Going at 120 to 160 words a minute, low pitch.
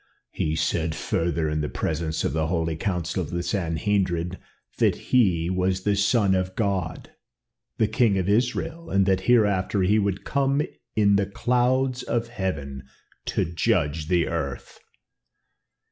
Yes: average, 145 wpm; very low, 95 Hz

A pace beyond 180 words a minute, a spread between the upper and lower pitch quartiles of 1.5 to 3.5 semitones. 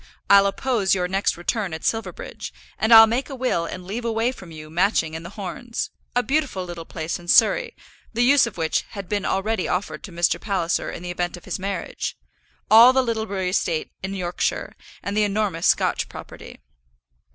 No: average, 190 wpm; average, 4.2 semitones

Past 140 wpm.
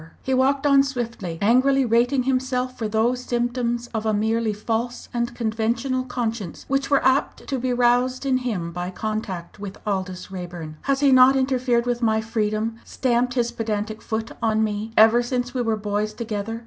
Yes: average, 175 wpm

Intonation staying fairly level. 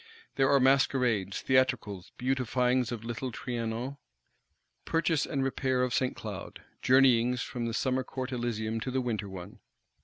Yes: narrow, 2.3 semitones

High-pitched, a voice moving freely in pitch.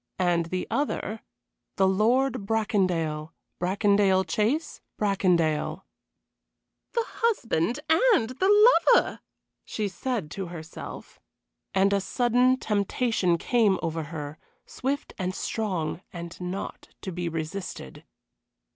Yes: high, 195 Hz; wide, 5.7 semitones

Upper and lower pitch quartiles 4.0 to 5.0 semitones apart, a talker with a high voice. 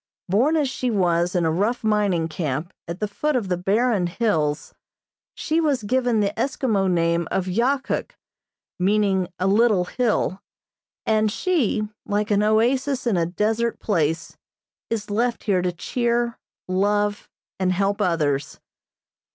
Yes: average, 4.7 semitones; high, 205 Hz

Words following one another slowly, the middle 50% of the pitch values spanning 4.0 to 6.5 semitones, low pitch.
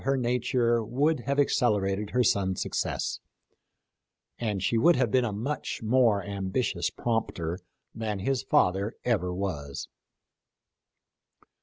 Yes: slow, 120 wpm; average, 4.3 semitones; low, 110 Hz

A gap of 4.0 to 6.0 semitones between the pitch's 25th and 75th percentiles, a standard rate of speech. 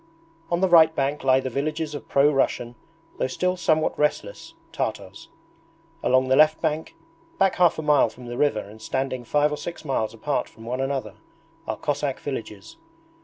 No: average, 3.3 semitones; average, 175 wpm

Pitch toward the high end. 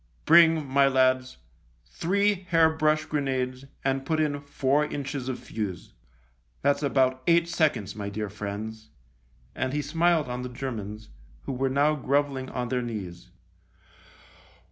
No: low, 135 Hz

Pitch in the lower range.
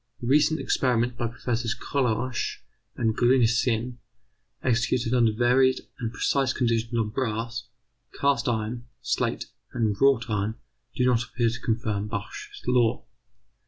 Yes: low, 120 Hz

